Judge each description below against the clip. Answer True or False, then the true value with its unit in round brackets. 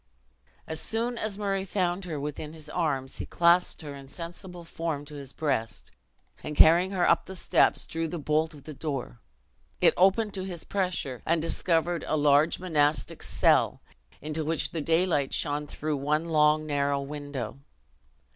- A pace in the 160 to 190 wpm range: True (165 wpm)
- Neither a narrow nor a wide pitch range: True (3.3 semitones)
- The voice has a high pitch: False (155 Hz)